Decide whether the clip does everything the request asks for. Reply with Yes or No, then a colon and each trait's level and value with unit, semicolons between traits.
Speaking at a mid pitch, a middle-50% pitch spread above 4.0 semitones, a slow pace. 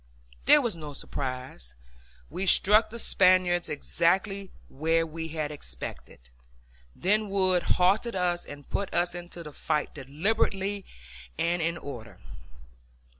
Yes: medium, 175 Hz; average, 4.6 semitones; slow, 125 wpm